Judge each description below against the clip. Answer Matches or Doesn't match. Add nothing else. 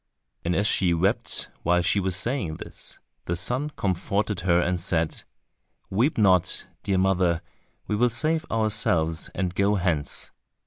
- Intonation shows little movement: Doesn't match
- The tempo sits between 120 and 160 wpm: Matches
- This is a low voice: Matches